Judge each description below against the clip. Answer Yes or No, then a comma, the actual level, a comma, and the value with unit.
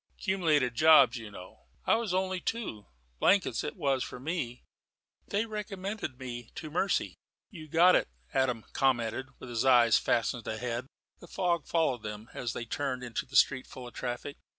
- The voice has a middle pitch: No, low, 130 Hz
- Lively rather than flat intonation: Yes, wide, 6.6 semitones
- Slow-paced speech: No, average, 170 wpm